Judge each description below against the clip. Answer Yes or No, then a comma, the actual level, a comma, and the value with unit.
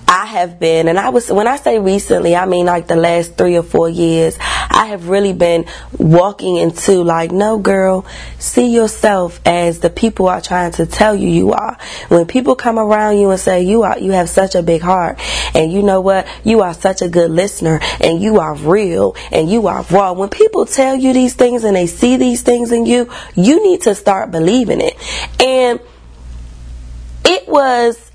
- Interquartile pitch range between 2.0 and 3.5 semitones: No, average, 5.1 semitones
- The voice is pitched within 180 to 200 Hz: Yes, high, 190 Hz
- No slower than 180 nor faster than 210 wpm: Yes, fast, 205 wpm